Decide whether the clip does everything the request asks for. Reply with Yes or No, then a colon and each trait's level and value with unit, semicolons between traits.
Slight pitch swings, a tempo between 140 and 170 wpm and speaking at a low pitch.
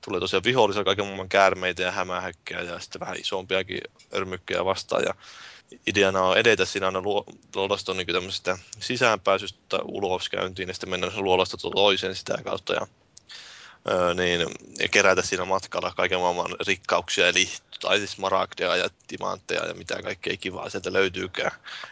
Yes: narrow, 1.1 semitones; average, 145 wpm; very low, 95 Hz